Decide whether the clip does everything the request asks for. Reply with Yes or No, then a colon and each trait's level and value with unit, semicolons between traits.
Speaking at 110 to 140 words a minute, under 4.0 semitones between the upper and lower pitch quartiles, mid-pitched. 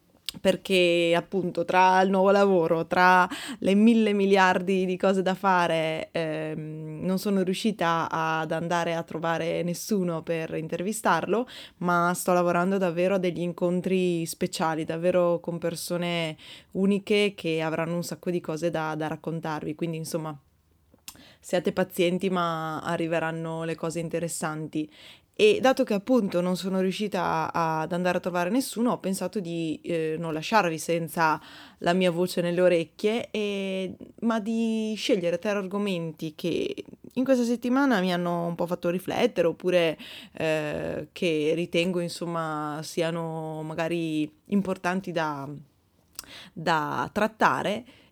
Yes: average, 130 wpm; narrow, 2.6 semitones; medium, 175 Hz